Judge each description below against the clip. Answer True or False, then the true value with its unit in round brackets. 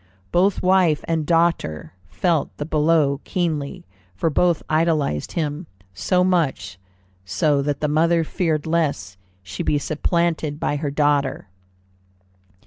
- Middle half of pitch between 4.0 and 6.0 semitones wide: False (2.8 semitones)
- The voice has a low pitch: False (155 Hz)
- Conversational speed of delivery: False (125 wpm)